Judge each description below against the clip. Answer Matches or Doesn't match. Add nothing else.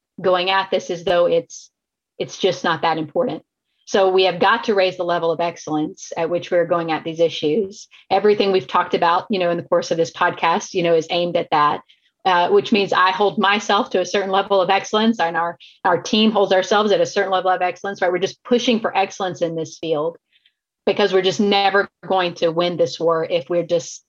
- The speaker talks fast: Matches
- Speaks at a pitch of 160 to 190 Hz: Matches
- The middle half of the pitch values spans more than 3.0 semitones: Doesn't match